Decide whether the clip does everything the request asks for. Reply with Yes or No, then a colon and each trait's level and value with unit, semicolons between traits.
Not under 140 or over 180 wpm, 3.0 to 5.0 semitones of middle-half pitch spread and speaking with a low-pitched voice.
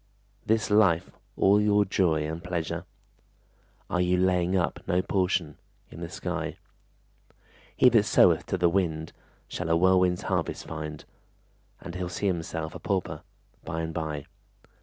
No: average, 145 wpm; narrow, 2.6 semitones; very low, 90 Hz